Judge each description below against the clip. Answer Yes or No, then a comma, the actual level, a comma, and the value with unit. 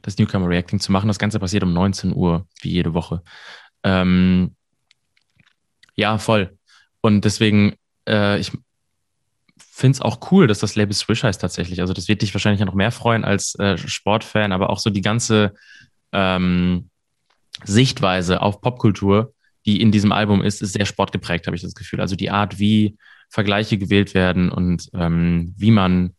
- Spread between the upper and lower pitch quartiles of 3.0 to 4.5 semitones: No, narrow, 2.5 semitones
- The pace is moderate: Yes, average, 170 wpm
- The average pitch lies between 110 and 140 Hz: No, low, 100 Hz